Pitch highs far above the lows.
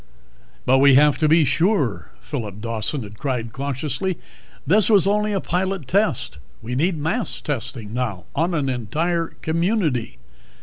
Yes: wide, 6.4 semitones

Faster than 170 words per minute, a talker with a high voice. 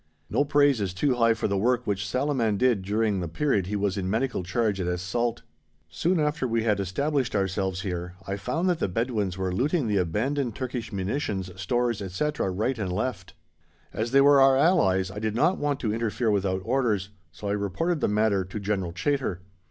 No: average, 200 wpm; low, 110 Hz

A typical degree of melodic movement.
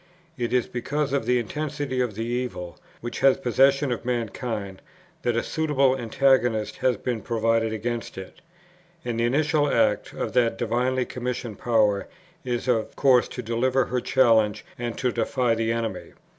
No: narrow, 2.3 semitones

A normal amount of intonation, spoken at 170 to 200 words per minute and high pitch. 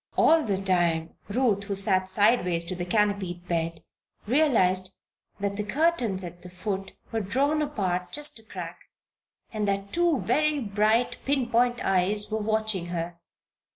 No: average, 4.6 semitones; average, 155 wpm; high, 200 Hz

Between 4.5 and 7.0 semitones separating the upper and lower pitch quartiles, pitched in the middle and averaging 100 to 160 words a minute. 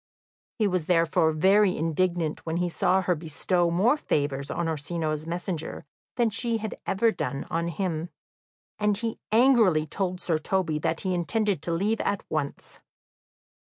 No: average, 3.9 semitones; medium, 175 Hz; average, 155 wpm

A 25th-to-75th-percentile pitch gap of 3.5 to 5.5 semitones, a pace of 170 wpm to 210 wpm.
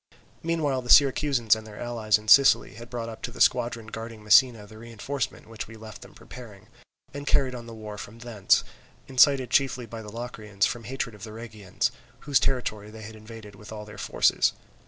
No: average, 2.7 semitones; average, 200 wpm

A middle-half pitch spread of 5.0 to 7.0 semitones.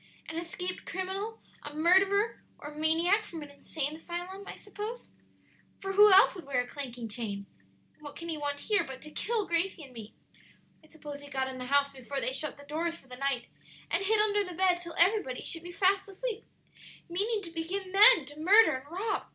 Yes: wide, 5.4 semitones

